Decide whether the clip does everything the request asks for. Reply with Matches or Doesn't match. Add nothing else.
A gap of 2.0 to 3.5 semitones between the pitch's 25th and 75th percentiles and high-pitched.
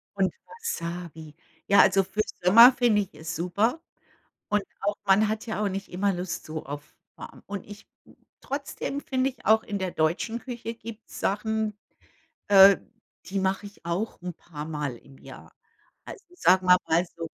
Doesn't match